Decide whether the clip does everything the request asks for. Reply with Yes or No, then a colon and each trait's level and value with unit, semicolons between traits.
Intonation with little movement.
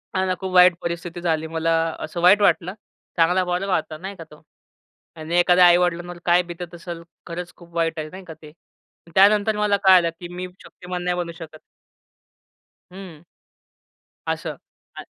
Yes: narrow, 1.6 semitones